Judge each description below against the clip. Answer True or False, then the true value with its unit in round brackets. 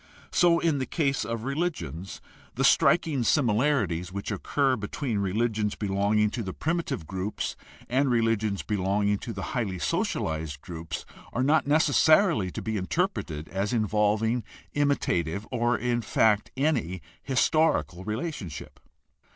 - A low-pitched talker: True (110 Hz)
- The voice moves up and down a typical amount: False (6.1 semitones)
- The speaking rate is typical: False (130 wpm)